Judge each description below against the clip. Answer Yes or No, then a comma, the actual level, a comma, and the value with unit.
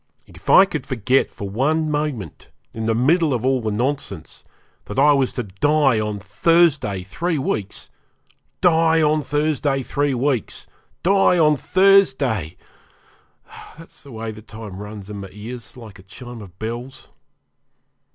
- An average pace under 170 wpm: Yes, average, 150 wpm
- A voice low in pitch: Yes, low, 130 Hz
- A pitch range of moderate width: No, wide, 6.0 semitones